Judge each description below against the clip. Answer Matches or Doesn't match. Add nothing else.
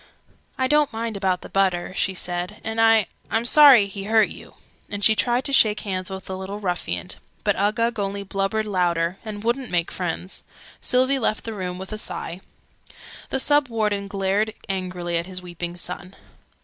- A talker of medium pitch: Doesn't match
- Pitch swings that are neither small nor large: Matches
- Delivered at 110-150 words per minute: Doesn't match